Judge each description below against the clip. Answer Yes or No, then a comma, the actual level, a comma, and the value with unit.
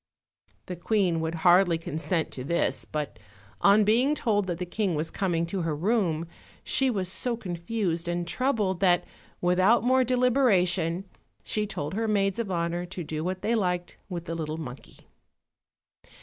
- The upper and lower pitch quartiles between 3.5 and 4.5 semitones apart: Yes, average, 4.0 semitones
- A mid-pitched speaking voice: Yes, medium, 180 Hz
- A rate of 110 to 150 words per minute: No, average, 165 wpm